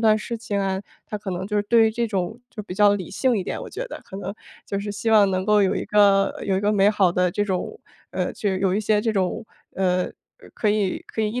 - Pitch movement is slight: Yes, narrow, 2.0 semitones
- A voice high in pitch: Yes, high, 205 Hz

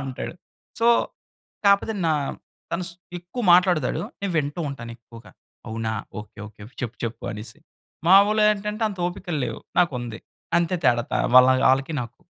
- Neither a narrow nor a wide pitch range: No, wide, 8.0 semitones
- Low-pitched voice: No, medium, 150 Hz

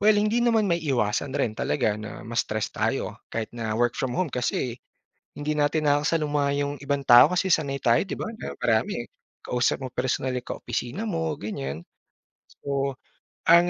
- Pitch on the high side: No, medium, 140 Hz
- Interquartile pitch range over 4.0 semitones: Yes, average, 4.9 semitones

